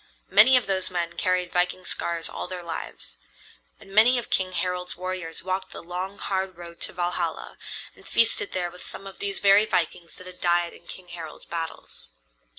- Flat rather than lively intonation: Yes, narrow, 1.7 semitones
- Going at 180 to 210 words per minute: Yes, average, 185 wpm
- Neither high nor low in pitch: Yes, medium, 180 Hz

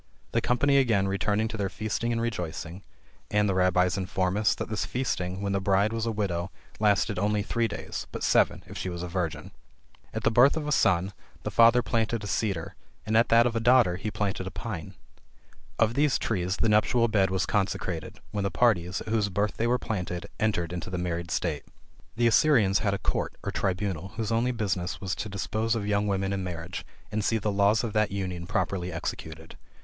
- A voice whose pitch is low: Yes, low, 100 Hz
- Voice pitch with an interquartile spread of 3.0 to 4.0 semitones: Yes, average, 3.5 semitones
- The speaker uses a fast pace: Yes, fast, 210 wpm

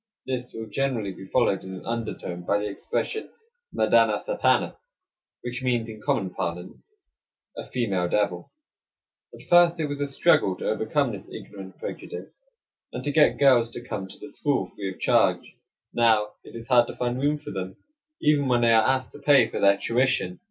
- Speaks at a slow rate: No, average, 185 wpm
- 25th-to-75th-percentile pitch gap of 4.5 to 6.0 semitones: Yes, average, 5.3 semitones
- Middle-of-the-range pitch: No, low, 120 Hz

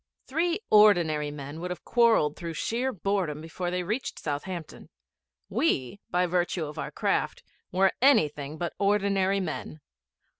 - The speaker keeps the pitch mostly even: No, average, 4.7 semitones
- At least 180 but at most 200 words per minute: No, average, 140 wpm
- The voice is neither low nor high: Yes, medium, 180 Hz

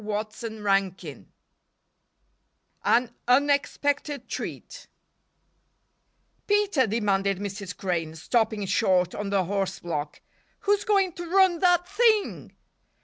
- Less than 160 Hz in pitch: No, high, 220 Hz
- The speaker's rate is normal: No, slow, 95 wpm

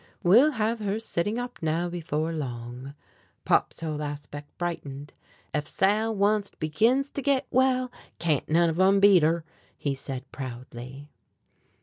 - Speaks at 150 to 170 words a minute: No, average, 140 wpm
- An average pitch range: No, wide, 6.6 semitones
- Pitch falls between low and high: Yes, medium, 165 Hz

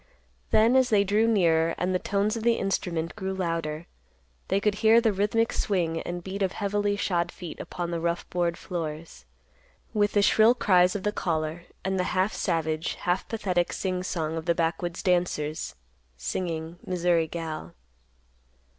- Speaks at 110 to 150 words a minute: No, average, 165 wpm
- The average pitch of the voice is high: No, medium, 180 Hz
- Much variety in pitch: No, average, 3.4 semitones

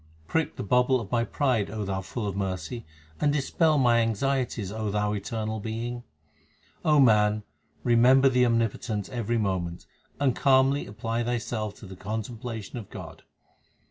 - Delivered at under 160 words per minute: Yes, average, 150 wpm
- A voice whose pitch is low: Yes, low, 115 Hz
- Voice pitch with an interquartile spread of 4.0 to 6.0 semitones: No, average, 3.2 semitones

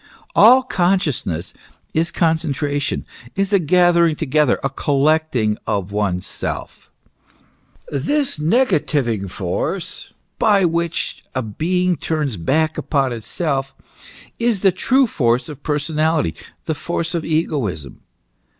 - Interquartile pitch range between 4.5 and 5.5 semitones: Yes, average, 5.1 semitones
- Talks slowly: Yes, slow, 110 wpm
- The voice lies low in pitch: No, medium, 155 Hz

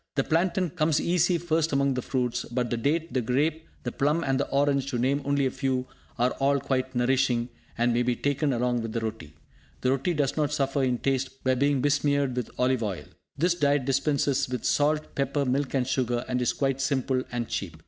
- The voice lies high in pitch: No, low, 135 Hz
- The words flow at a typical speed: No, fast, 210 wpm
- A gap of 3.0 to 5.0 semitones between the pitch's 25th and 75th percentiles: No, narrow, 2.4 semitones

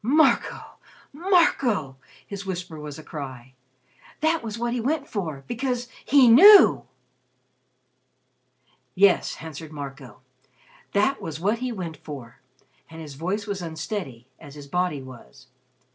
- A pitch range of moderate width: No, wide, 8.6 semitones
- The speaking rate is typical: No, slow, 130 wpm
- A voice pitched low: No, medium, 180 Hz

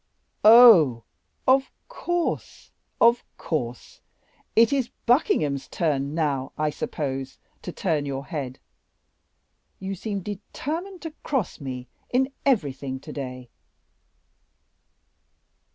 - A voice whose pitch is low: No, medium, 160 Hz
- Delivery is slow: Yes, slow, 100 wpm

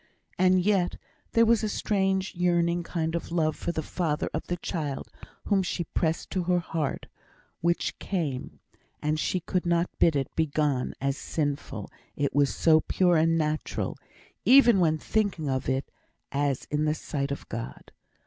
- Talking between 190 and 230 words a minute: No, average, 165 wpm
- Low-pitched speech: No, medium, 165 Hz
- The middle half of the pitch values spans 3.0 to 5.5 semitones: Yes, average, 3.4 semitones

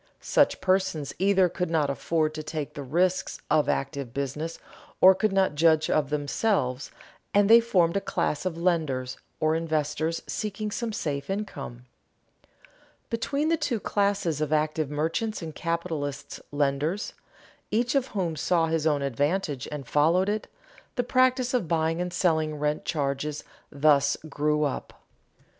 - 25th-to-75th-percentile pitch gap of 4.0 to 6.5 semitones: Yes, average, 4.4 semitones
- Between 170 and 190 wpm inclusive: No, average, 150 wpm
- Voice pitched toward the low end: No, medium, 160 Hz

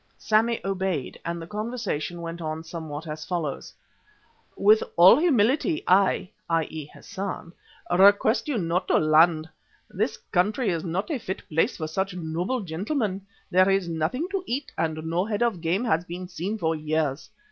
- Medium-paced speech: Yes, average, 160 wpm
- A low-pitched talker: No, medium, 180 Hz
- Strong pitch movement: No, average, 4.5 semitones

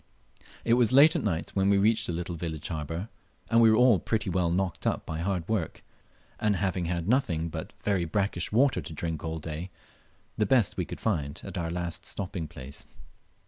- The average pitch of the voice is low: Yes, very low, 90 Hz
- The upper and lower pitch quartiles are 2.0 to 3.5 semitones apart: No, average, 4.5 semitones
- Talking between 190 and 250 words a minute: Yes, average, 200 wpm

